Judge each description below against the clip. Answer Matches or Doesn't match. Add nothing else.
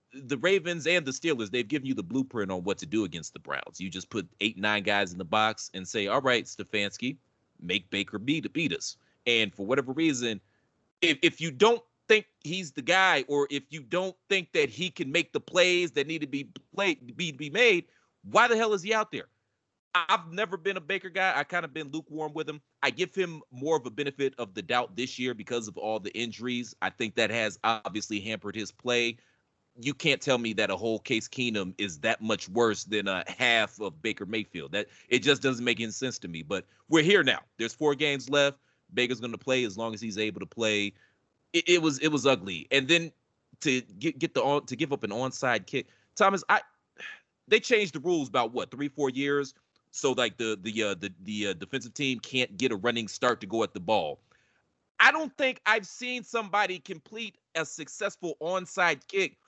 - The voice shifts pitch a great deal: Matches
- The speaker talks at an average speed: Doesn't match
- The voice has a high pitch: Doesn't match